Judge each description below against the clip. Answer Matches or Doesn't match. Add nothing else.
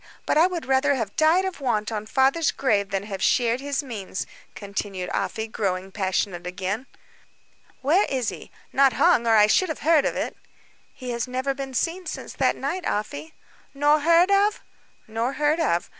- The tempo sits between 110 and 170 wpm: Doesn't match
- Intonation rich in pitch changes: Matches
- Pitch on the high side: Matches